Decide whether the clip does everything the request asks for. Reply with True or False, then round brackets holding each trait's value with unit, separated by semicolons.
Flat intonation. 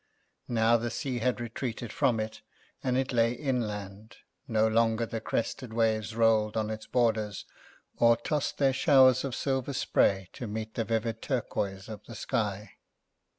True (2.3 semitones)